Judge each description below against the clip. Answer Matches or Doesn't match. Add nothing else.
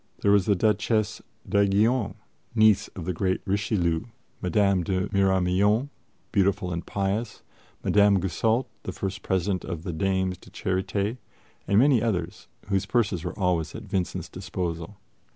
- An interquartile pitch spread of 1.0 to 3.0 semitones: Matches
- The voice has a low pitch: Matches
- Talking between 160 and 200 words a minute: Doesn't match